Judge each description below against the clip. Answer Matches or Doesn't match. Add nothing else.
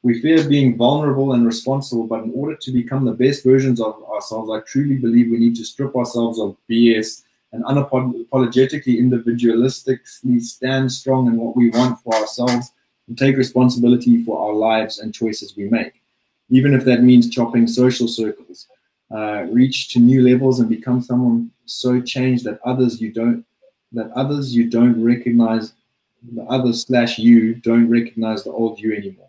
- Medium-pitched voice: Doesn't match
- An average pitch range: Doesn't match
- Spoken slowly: Doesn't match